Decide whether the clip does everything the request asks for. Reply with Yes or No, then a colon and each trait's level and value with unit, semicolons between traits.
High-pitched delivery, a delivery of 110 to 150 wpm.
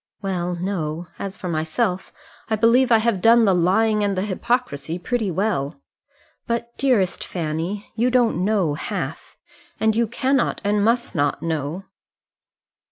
Yes: high, 200 Hz; average, 145 wpm